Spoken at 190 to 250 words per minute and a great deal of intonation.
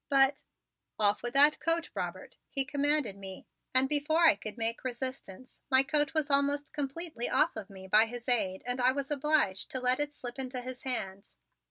No: average, 195 wpm; average, 3.9 semitones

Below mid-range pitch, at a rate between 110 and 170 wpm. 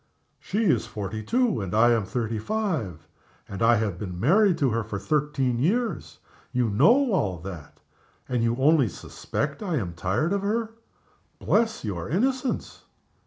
Yes: low, 125 Hz; average, 160 wpm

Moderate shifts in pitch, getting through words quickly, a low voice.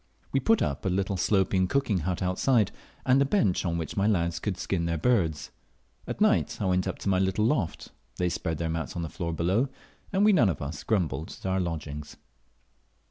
Yes: average, 4.2 semitones; fast, 210 wpm; very low, 95 Hz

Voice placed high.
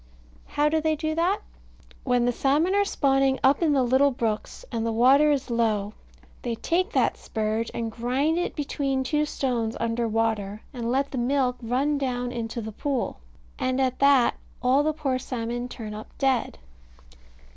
Yes: very high, 255 Hz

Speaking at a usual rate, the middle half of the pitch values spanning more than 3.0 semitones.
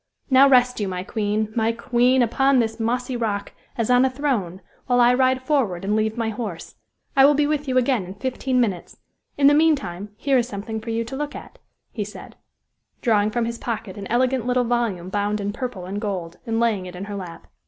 No: fast, 215 wpm; average, 3.9 semitones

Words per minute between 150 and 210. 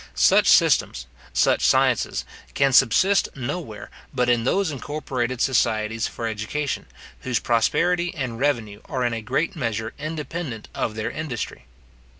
No: slow, 135 wpm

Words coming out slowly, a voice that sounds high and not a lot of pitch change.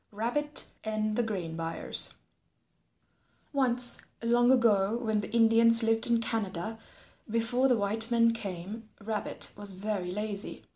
Yes: slow, 130 wpm; high, 225 Hz; narrow, 2.3 semitones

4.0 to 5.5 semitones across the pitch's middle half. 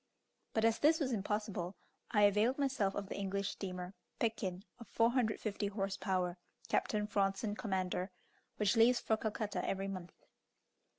No: narrow, 2.4 semitones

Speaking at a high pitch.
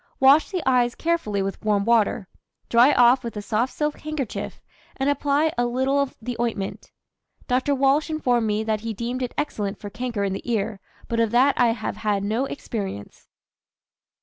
Yes: high, 240 Hz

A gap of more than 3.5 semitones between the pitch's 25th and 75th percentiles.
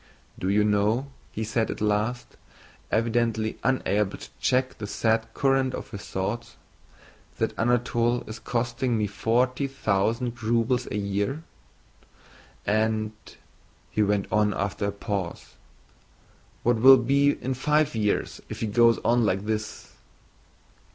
No: average, 2.9 semitones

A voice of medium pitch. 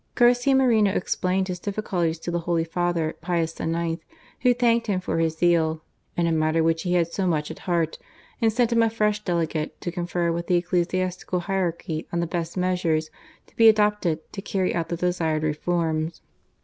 Yes: medium, 175 Hz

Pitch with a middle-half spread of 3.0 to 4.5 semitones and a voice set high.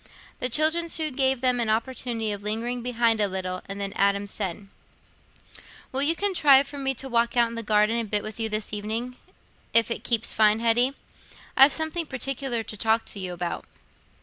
Yes: average, 3.9 semitones; high, 230 Hz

